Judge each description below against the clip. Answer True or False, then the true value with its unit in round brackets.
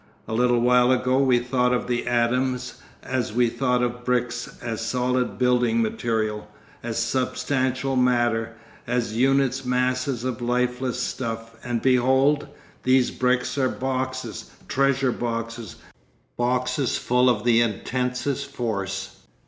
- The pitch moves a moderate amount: False (1.5 semitones)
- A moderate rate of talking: False (125 wpm)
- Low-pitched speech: True (125 Hz)